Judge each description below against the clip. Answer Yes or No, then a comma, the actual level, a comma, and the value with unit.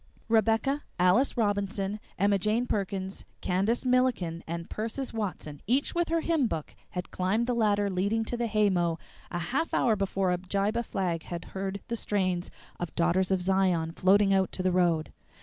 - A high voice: Yes, high, 195 Hz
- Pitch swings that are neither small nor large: Yes, average, 3.7 semitones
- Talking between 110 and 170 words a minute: Yes, average, 165 wpm